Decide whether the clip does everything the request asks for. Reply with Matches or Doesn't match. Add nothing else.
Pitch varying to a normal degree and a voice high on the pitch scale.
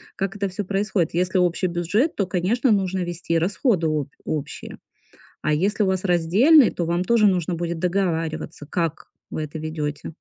Doesn't match